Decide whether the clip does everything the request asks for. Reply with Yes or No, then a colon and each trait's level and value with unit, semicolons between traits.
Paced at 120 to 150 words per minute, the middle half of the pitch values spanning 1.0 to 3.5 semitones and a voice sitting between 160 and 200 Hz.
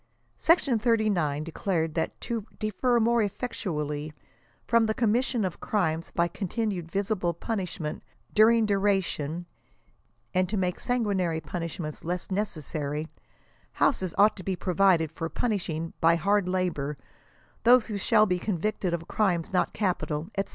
No: average, 145 wpm; average, 4.4 semitones; medium, 185 Hz